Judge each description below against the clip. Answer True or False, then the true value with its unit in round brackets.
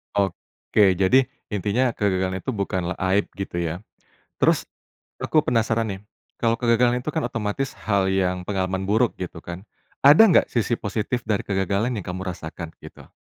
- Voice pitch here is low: True (100 Hz)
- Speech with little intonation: False (3.7 semitones)